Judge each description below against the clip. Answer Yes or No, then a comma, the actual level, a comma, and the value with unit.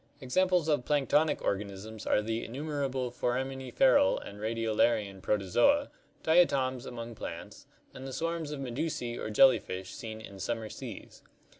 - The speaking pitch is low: Yes, low, 125 Hz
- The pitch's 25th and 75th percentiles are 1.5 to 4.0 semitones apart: No, average, 5.2 semitones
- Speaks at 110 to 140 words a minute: Yes, slow, 135 wpm